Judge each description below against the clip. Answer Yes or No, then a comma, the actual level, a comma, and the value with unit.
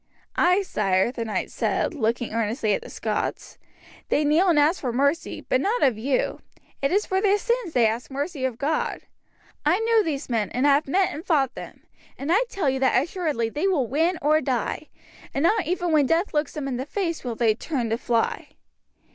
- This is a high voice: Yes, very high, 290 Hz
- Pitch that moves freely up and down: Yes, wide, 5.9 semitones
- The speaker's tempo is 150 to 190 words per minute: No, fast, 205 wpm